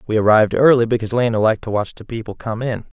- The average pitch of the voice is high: No, low, 115 Hz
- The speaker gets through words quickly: Yes, fast, 240 wpm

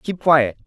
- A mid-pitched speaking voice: Yes, medium, 145 Hz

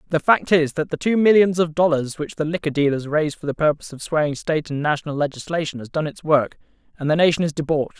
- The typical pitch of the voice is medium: Yes, medium, 155 Hz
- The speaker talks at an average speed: No, fast, 240 wpm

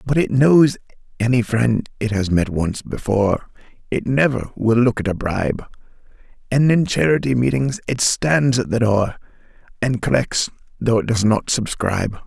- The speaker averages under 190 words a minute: Yes, average, 155 wpm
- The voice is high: No, low, 120 Hz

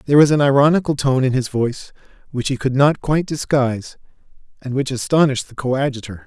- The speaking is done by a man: Yes, male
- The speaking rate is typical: Yes, average, 180 wpm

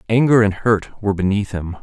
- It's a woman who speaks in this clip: No, male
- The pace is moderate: Yes, average, 195 wpm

